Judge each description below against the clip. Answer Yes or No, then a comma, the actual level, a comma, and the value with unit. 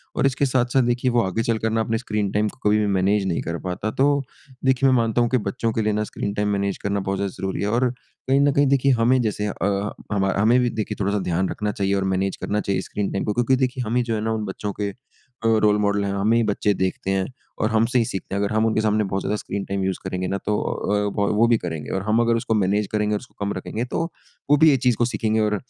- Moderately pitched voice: No, low, 105 Hz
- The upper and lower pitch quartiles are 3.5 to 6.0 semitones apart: No, average, 2.9 semitones